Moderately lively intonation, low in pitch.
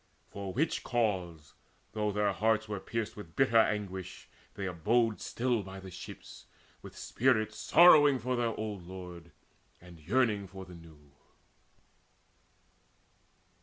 Yes: average, 3.9 semitones; low, 105 Hz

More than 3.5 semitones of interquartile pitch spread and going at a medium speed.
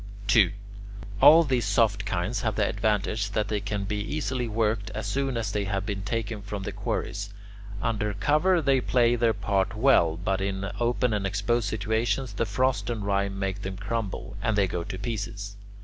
No: average, 2.8 semitones; average, 185 wpm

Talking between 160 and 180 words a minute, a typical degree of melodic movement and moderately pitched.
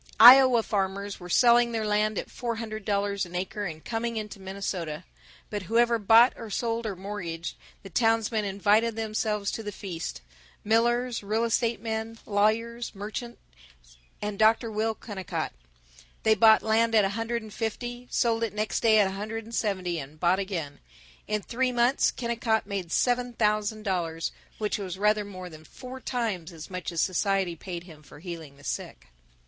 No: average, 175 wpm; average, 3.1 semitones; high, 210 Hz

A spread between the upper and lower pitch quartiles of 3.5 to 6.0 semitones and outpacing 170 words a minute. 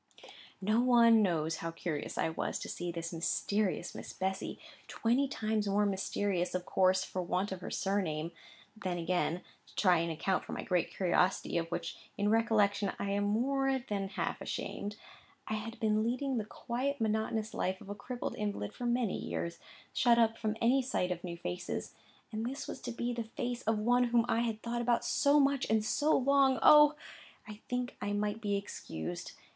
Yes: average, 4.4 semitones; average, 185 wpm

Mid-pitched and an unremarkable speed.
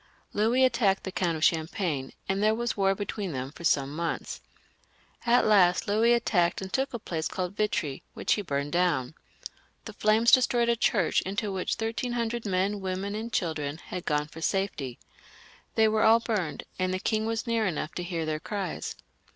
No: high, 195 Hz; average, 185 wpm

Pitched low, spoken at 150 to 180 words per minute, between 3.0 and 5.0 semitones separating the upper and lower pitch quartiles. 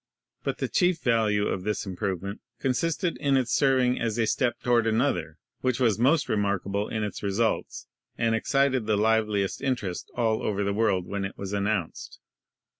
Yes: low, 110 Hz; average, 175 wpm; average, 3.8 semitones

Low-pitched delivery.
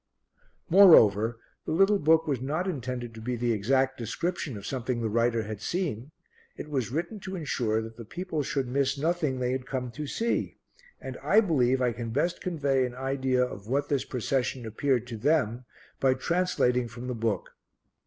Yes: low, 130 Hz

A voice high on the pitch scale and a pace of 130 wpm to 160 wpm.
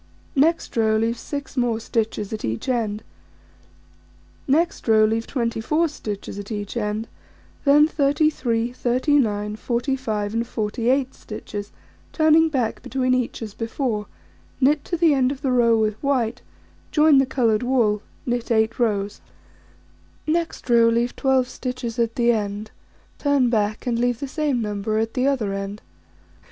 Yes: high, 235 Hz; average, 145 wpm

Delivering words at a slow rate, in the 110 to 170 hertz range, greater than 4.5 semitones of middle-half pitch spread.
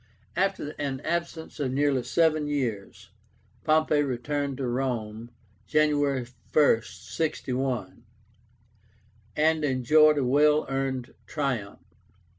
No: slow, 95 wpm; medium, 140 Hz; average, 3.0 semitones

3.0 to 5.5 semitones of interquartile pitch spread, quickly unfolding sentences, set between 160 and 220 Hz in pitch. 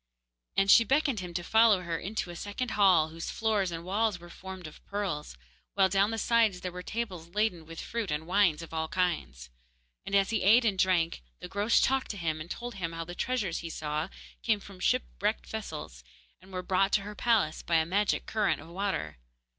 Yes: average, 4.0 semitones; fast, 210 wpm; medium, 185 Hz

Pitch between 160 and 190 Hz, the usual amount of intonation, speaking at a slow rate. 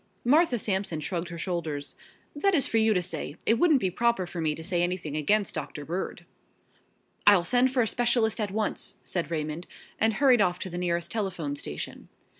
No: medium, 185 Hz; average, 4.9 semitones; average, 195 wpm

